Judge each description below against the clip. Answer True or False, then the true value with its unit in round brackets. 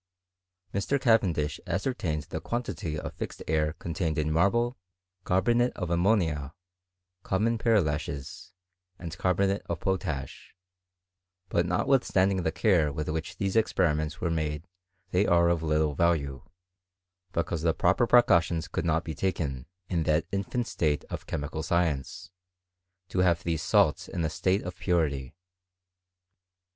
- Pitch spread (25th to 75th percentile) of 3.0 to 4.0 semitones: True (3.7 semitones)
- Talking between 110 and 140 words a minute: True (135 wpm)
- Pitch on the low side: True (85 Hz)